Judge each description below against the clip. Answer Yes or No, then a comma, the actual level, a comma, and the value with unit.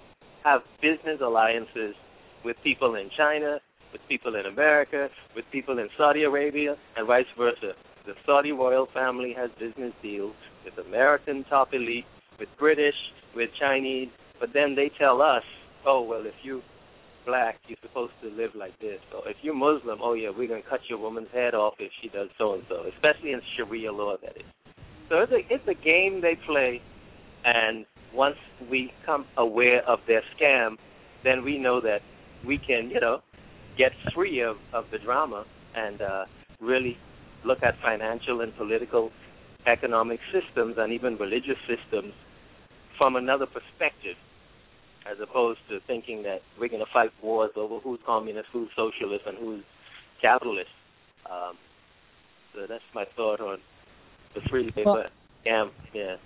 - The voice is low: Yes, low, 130 Hz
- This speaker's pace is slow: No, average, 160 wpm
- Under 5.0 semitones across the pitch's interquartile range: Yes, average, 4.6 semitones